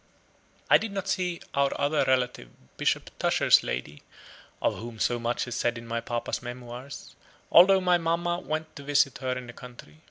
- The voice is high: No, low, 130 Hz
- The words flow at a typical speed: Yes, average, 180 wpm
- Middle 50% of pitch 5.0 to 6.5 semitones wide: Yes, wide, 5.6 semitones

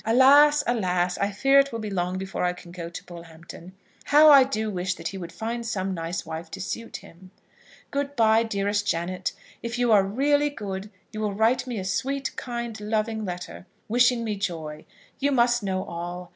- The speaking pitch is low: No, high, 210 Hz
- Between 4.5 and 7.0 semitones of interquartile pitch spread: Yes, average, 5.0 semitones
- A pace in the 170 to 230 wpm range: Yes, average, 195 wpm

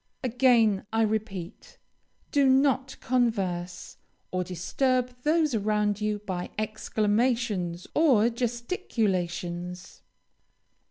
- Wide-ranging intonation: No, average, 4.9 semitones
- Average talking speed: No, slow, 85 wpm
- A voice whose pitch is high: Yes, high, 215 Hz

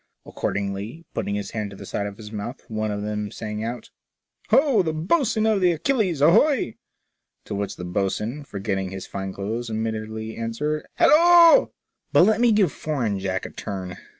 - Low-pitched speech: Yes, low, 110 Hz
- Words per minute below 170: No, average, 180 wpm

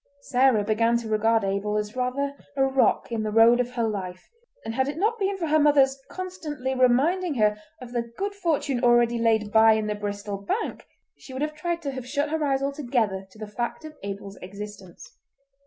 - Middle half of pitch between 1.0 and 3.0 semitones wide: No, average, 5.2 semitones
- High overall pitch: Yes, high, 240 Hz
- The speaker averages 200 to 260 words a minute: Yes, fast, 205 wpm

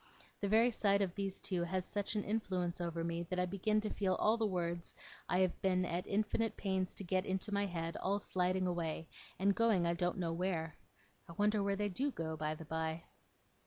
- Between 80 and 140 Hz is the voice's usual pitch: No, medium, 185 Hz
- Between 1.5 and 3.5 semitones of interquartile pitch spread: Yes, average, 2.8 semitones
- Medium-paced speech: No, fast, 210 wpm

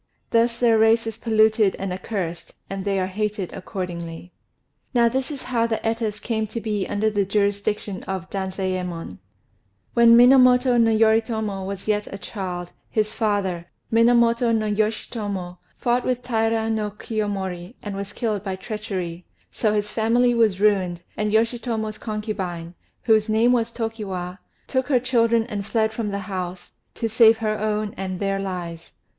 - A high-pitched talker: Yes, high, 215 Hz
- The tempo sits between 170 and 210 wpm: No, average, 155 wpm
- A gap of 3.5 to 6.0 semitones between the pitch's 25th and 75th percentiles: No, average, 3.0 semitones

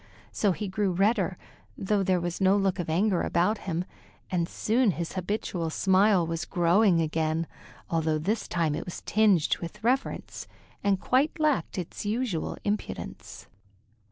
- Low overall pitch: No, medium, 185 Hz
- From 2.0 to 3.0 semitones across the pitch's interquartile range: No, average, 3.7 semitones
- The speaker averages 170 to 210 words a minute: No, average, 150 wpm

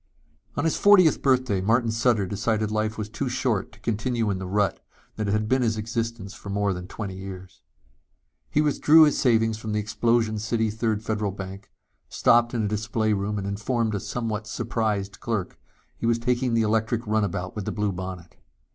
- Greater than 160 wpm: Yes, average, 185 wpm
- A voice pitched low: Yes, low, 110 Hz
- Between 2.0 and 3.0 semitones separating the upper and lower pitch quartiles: Yes, narrow, 2.5 semitones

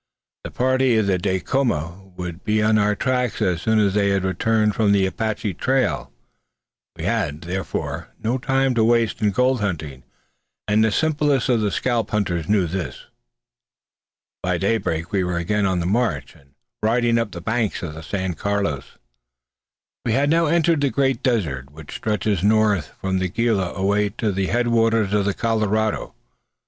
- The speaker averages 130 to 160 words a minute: No, average, 170 wpm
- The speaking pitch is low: Yes, low, 105 Hz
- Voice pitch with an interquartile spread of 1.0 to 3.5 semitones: No, average, 3.9 semitones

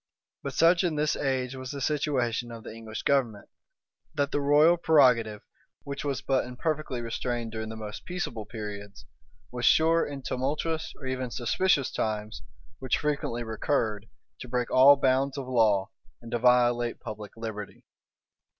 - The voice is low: Yes, low, 125 Hz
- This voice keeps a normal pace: Yes, average, 155 wpm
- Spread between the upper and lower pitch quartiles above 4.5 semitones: No, average, 4.0 semitones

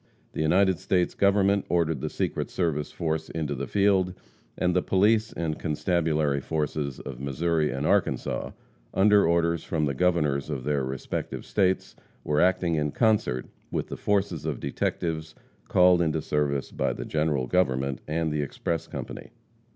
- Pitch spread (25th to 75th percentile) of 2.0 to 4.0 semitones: Yes, average, 3.7 semitones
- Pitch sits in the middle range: No, very low, 80 Hz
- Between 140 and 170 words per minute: Yes, average, 155 wpm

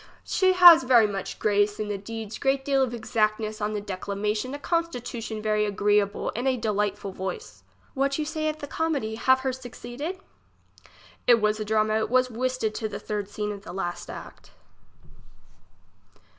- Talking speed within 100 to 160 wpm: No, average, 180 wpm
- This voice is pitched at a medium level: No, high, 220 Hz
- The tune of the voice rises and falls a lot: No, average, 3.9 semitones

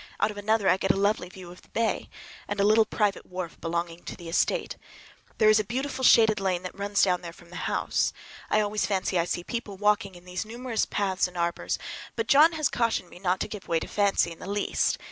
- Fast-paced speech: Yes, fast, 240 wpm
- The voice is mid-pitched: No, high, 200 Hz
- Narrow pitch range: No, average, 3.2 semitones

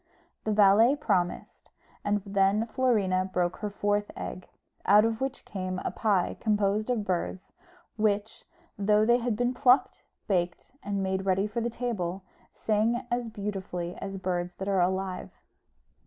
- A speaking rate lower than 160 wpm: Yes, average, 150 wpm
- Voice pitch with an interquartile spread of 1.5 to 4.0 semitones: Yes, average, 2.8 semitones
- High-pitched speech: Yes, high, 205 Hz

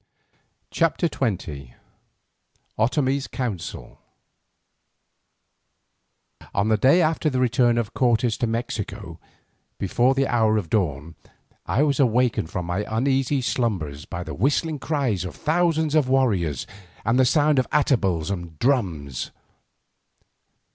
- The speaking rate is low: Yes, slow, 120 wpm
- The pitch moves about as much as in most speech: No, wide, 6.2 semitones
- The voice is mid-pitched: No, low, 120 Hz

